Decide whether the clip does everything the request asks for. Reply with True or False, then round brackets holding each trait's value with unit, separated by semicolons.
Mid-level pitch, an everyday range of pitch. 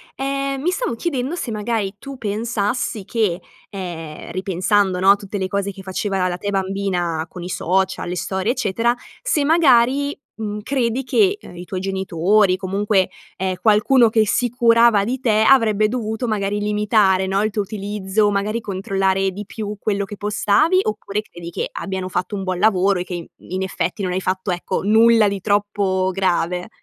False (205 Hz; 3.0 semitones)